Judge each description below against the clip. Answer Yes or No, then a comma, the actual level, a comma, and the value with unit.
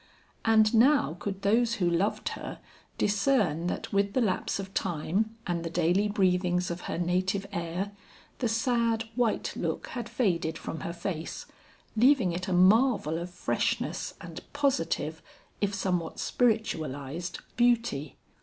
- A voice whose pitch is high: Yes, high, 195 Hz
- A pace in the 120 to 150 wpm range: Yes, average, 140 wpm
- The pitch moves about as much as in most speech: Yes, average, 4.7 semitones